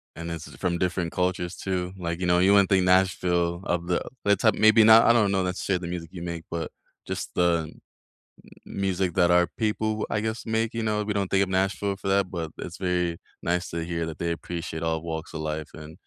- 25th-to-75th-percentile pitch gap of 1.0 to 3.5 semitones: Yes, narrow, 2.6 semitones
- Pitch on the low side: Yes, very low, 90 Hz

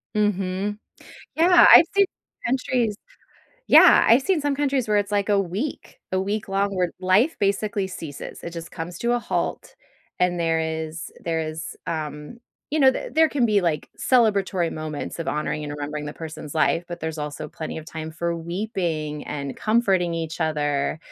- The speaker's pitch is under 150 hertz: No, medium, 175 Hz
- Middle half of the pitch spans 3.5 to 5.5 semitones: Yes, average, 4.9 semitones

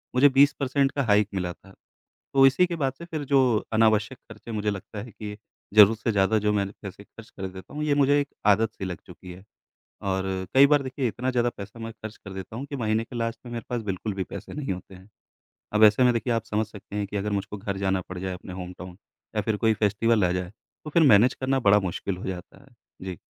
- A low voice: Yes, low, 110 Hz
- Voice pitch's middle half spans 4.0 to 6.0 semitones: Yes, average, 4.6 semitones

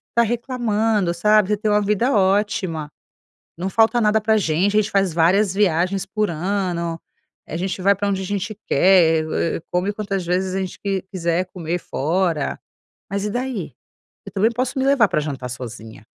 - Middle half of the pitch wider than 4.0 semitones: No, average, 3.6 semitones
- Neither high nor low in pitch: No, high, 195 Hz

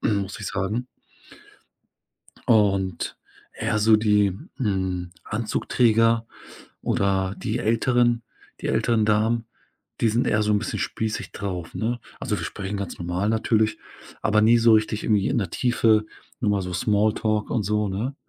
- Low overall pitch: Yes, low, 105 Hz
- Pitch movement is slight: Yes, narrow, 2.3 semitones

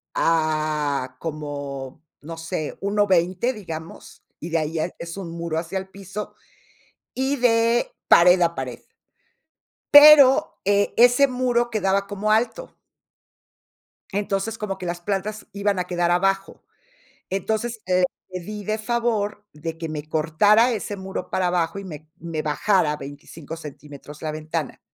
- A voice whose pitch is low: No, medium, 185 Hz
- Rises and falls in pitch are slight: No, average, 4.9 semitones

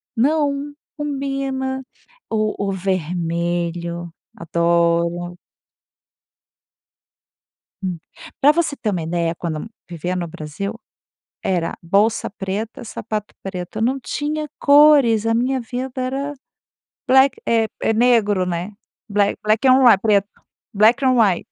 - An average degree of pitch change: No, wide, 7.0 semitones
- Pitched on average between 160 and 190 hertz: No, high, 215 Hz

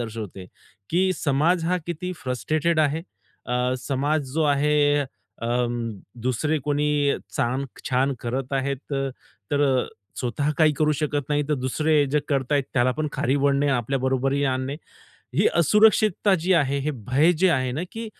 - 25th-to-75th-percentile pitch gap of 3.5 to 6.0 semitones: No, average, 2.9 semitones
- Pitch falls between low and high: Yes, medium, 145 Hz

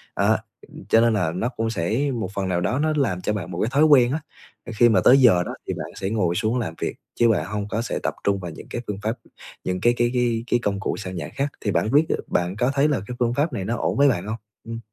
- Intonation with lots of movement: No, average, 4.4 semitones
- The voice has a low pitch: Yes, low, 115 Hz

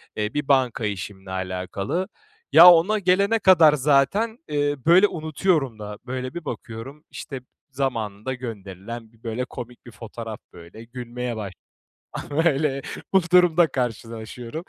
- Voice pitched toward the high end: No, low, 130 Hz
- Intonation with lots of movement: Yes, wide, 6.0 semitones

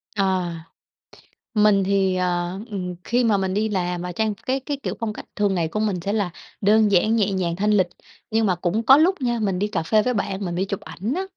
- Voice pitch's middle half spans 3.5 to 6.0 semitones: No, average, 3.1 semitones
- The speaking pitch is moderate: No, high, 200 Hz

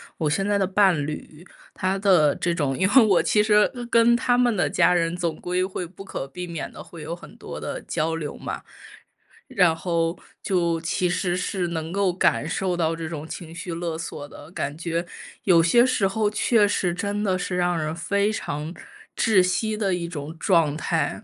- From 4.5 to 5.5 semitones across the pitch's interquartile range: No, average, 3.1 semitones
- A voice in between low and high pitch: Yes, medium, 175 Hz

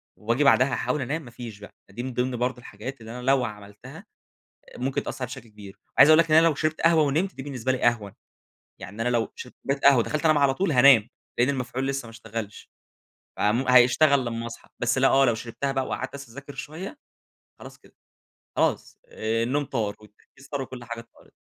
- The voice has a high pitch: No, low, 125 Hz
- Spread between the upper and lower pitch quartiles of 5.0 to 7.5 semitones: No, average, 3.3 semitones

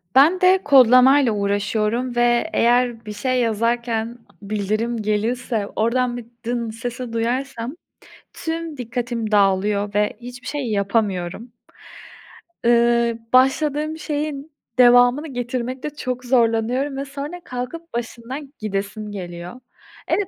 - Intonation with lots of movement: No, average, 3.1 semitones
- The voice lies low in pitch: No, high, 240 Hz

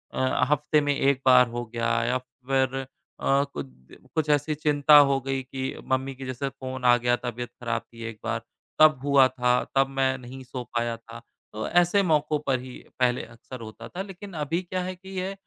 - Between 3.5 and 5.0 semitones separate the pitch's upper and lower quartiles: No, average, 3.0 semitones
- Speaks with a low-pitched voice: Yes, low, 130 Hz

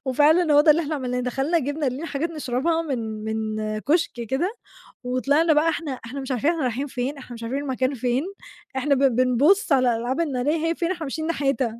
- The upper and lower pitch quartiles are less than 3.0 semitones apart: No, average, 4.0 semitones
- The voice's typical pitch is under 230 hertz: No, very high, 275 Hz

